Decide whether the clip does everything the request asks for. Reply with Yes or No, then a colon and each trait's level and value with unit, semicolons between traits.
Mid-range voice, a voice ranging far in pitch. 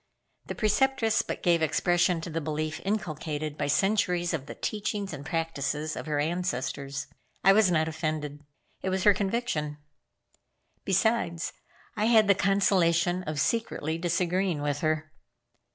No: medium, 170 Hz; average, 4.1 semitones